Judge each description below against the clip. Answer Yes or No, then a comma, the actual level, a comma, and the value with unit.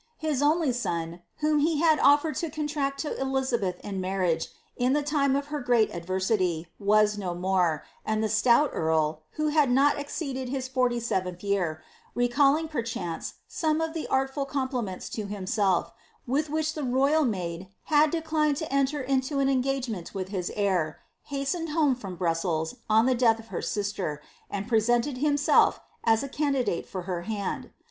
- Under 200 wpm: Yes, average, 170 wpm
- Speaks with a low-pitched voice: No, high, 245 Hz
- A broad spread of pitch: Yes, wide, 7.1 semitones